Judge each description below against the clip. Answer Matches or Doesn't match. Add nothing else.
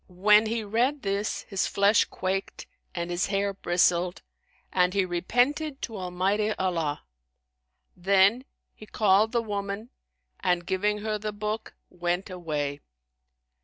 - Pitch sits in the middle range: Doesn't match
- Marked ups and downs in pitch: Doesn't match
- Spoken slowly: Matches